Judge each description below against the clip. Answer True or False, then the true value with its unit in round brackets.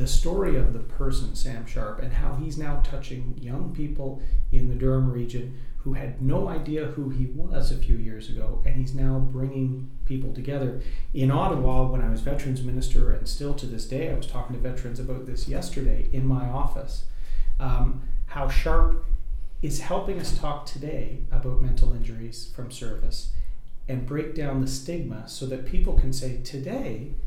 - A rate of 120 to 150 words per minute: False (180 wpm)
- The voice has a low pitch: True (130 Hz)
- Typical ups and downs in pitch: False (1.7 semitones)